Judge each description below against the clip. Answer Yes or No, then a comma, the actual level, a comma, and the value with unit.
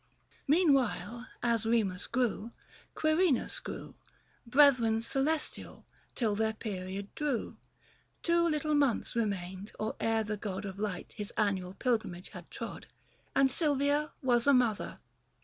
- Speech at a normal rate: No, slow, 130 wpm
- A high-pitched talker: Yes, high, 230 Hz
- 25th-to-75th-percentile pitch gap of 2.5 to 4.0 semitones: No, wide, 5.5 semitones